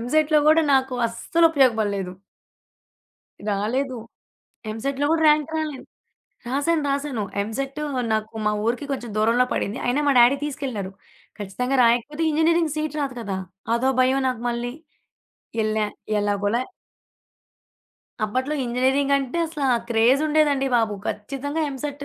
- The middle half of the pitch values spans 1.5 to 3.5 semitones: No, average, 4.2 semitones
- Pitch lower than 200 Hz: No, very high, 265 Hz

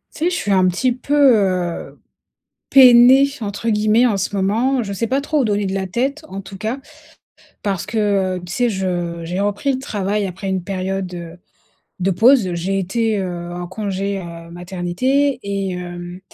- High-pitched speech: Yes, high, 195 Hz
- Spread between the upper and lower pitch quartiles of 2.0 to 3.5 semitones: No, average, 4.3 semitones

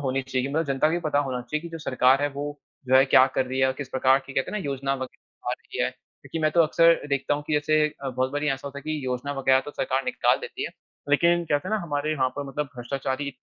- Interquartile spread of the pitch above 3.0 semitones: No, narrow, 2.5 semitones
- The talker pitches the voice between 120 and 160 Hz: Yes, medium, 140 Hz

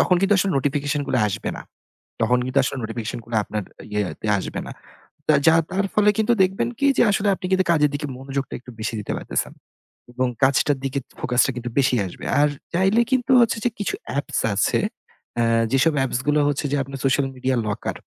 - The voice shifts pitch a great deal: Yes, wide, 6.6 semitones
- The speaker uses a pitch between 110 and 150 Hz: Yes, medium, 140 Hz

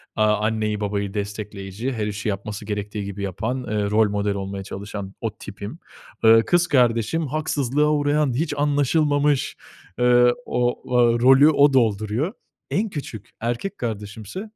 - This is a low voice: Yes, low, 115 Hz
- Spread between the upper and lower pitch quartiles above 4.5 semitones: Yes, wide, 5.5 semitones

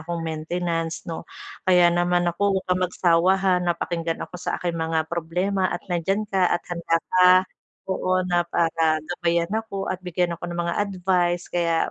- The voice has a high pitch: No, medium, 175 Hz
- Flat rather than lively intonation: Yes, narrow, 1.6 semitones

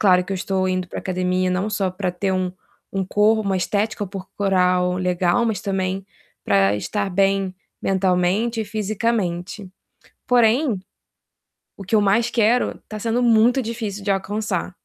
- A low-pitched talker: No, high, 195 Hz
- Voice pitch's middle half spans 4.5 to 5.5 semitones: No, average, 2.8 semitones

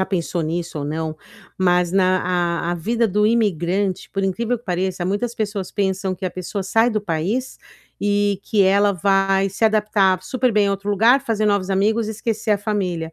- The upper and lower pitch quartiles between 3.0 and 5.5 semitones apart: No, narrow, 2.6 semitones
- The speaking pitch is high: Yes, high, 195 Hz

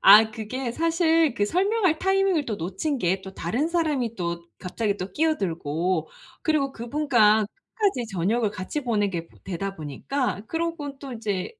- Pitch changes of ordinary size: No, wide, 8.3 semitones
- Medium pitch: No, high, 230 Hz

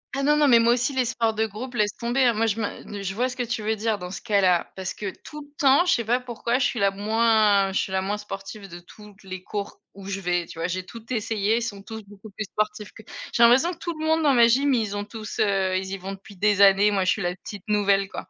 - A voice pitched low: No, high, 210 Hz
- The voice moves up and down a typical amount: Yes, average, 3.2 semitones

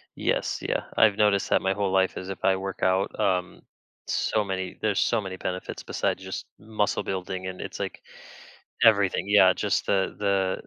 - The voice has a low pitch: Yes, very low, 95 Hz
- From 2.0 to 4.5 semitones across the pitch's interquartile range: No, narrow, 1.5 semitones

